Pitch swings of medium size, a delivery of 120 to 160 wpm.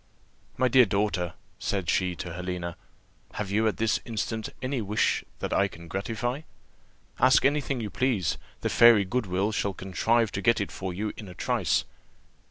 No: average, 4.0 semitones; average, 175 wpm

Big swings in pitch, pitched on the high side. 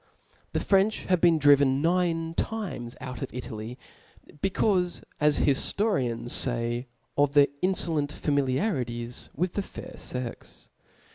No: wide, 6.3 semitones; medium, 145 Hz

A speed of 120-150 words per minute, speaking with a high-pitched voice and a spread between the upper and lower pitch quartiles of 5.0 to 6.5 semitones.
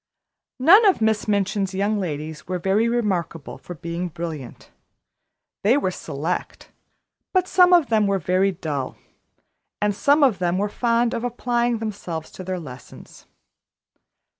Yes: average, 140 wpm; high, 195 Hz; average, 5.3 semitones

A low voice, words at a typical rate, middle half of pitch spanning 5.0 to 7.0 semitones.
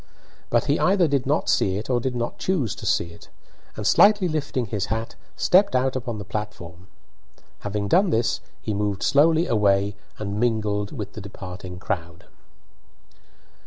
Yes: low, 110 Hz; average, 160 wpm; wide, 5.4 semitones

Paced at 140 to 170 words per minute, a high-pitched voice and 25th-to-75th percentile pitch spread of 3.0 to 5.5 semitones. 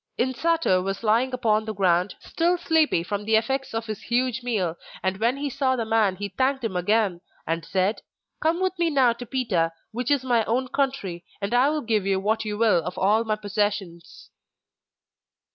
No: average, 195 wpm; high, 220 Hz; average, 4.8 semitones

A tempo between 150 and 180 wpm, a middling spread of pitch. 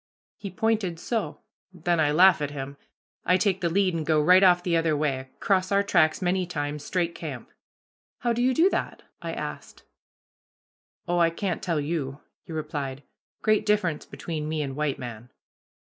Yes: average, 175 wpm; average, 3.9 semitones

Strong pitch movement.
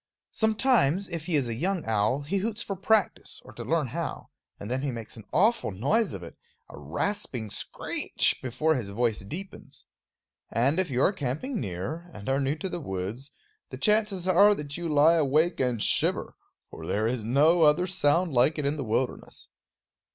Yes: wide, 7.3 semitones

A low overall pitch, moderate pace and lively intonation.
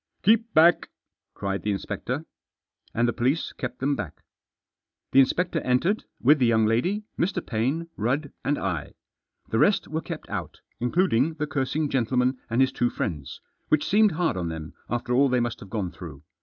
Yes: low, 130 Hz; average, 185 wpm; wide, 5.9 semitones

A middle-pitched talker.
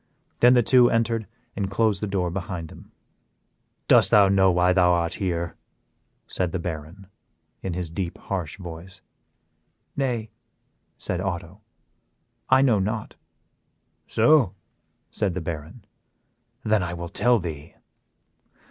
No: very low, 95 Hz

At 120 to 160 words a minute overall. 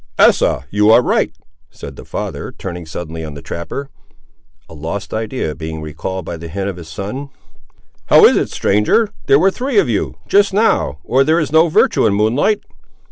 No: average, 190 wpm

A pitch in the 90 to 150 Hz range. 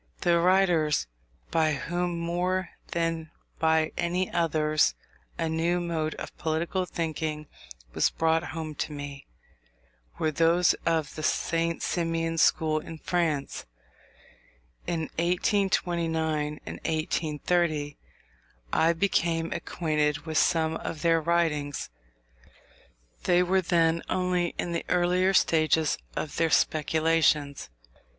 No: medium, 165 Hz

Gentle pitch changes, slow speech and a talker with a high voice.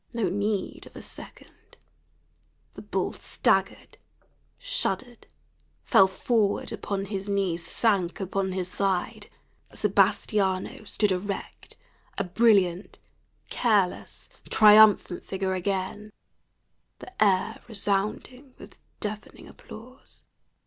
Yes: narrow, 2.3 semitones; slow, 95 wpm; high, 200 Hz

